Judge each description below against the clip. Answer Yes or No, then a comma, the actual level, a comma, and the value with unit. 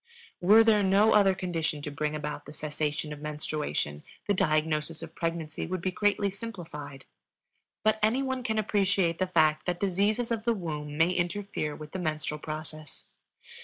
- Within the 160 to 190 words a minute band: Yes, average, 165 wpm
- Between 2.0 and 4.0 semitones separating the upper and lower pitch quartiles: No, average, 5.0 semitones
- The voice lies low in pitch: No, medium, 170 Hz